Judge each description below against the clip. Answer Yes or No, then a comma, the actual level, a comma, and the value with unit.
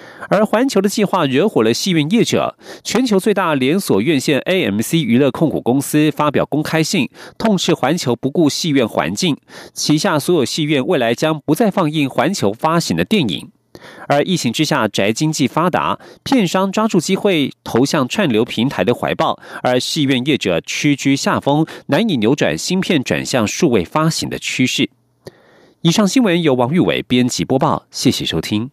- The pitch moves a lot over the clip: Yes, wide, 5.9 semitones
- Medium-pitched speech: Yes, medium, 155 Hz